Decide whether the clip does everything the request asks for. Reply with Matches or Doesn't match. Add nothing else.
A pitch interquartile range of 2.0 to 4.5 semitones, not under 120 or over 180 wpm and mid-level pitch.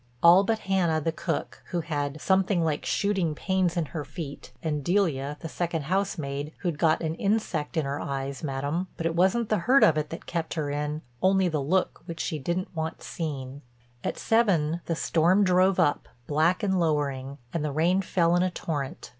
Doesn't match